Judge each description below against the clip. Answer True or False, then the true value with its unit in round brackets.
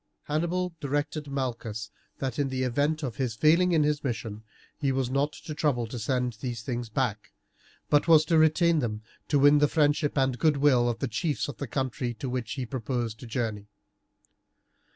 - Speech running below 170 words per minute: False (185 wpm)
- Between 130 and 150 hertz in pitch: True (135 Hz)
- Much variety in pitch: False (3.7 semitones)